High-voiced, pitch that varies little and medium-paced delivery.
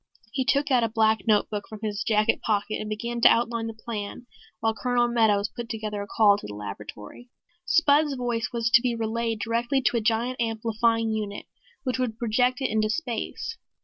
Yes: high, 225 Hz; narrow, 2.1 semitones; average, 190 wpm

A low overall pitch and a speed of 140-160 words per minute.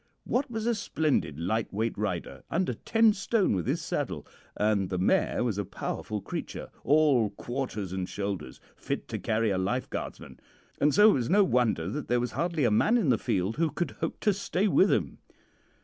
No: low, 120 Hz; average, 190 wpm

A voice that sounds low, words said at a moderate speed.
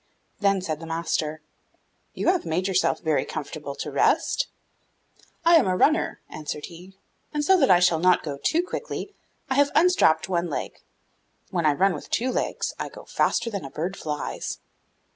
No: medium, 180 Hz; average, 180 wpm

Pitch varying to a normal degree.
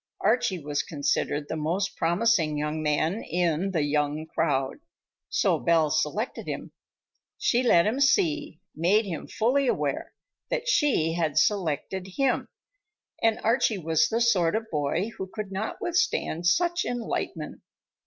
No: wide, 6.5 semitones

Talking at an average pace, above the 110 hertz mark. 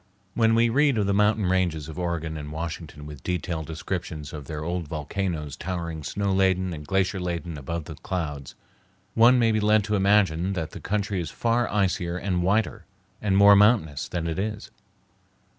No: average, 180 wpm; very low, 90 Hz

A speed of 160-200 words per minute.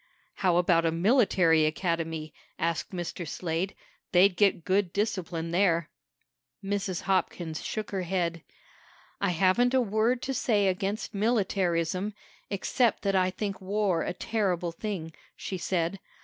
No: slow, 135 wpm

